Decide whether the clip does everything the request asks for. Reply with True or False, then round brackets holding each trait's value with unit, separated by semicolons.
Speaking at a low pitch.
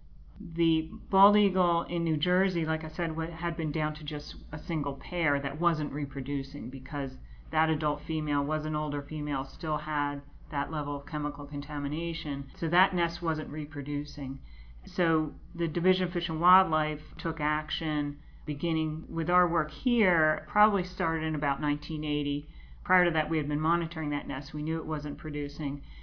False (155 Hz)